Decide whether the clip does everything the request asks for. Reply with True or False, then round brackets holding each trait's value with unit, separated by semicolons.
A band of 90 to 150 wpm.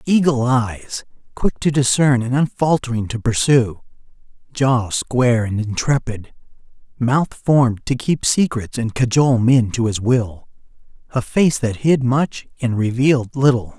True (135 wpm)